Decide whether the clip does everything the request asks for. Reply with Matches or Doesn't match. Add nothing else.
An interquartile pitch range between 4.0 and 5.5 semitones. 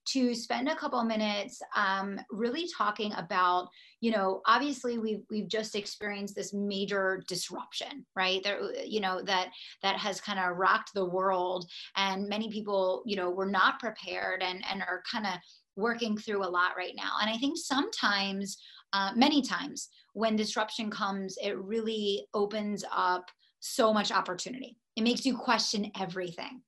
Doesn't match